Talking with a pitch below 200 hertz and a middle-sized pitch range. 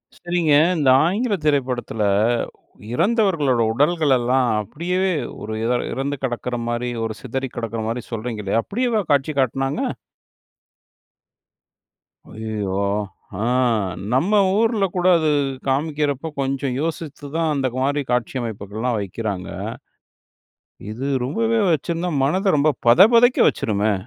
No: low, 135 Hz; wide, 6.2 semitones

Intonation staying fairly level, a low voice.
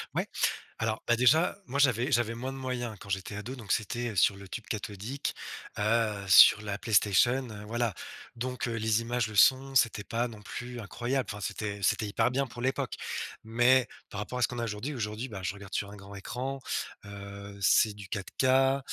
No: average, 3.4 semitones; low, 115 Hz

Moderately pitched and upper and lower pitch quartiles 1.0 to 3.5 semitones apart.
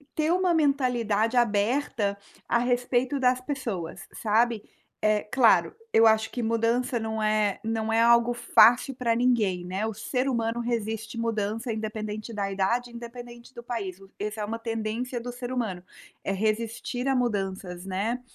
No: high, 230 Hz; narrow, 2.4 semitones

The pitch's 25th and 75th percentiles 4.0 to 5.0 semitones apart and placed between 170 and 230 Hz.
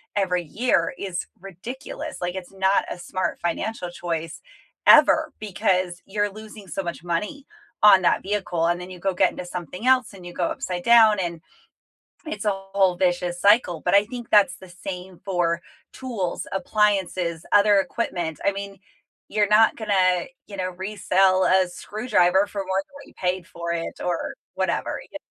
No: average, 2.8 semitones; high, 190 Hz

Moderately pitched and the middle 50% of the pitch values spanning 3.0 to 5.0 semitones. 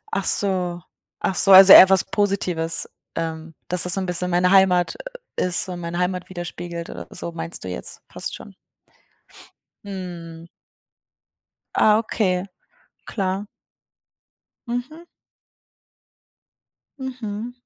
No: medium, 180 Hz; narrow, 2.4 semitones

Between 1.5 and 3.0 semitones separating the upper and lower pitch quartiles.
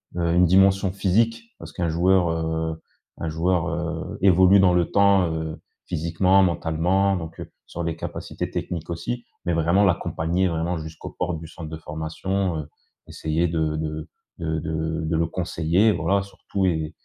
Yes: narrow, 2.6 semitones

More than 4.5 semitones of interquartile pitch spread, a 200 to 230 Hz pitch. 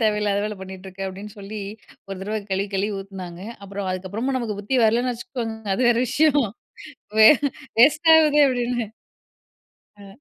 No: average, 3.8 semitones; high, 210 Hz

